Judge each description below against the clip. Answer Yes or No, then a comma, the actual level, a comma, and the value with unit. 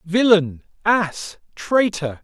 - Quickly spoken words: No, slow, 80 wpm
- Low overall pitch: No, medium, 185 Hz